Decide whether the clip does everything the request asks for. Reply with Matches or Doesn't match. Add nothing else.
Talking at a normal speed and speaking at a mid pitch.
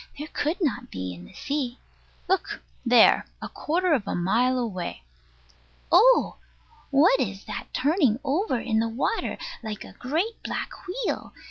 Doesn't match